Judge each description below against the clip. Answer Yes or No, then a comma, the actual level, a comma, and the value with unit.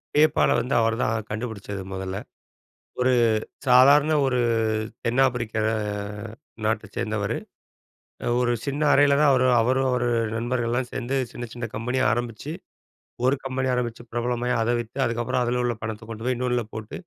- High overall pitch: No, low, 120 Hz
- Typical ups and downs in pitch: No, narrow, 2.1 semitones